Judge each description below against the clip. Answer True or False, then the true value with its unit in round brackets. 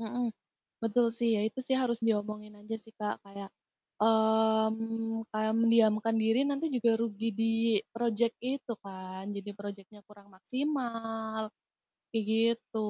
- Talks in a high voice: True (225 Hz)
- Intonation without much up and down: True (1.6 semitones)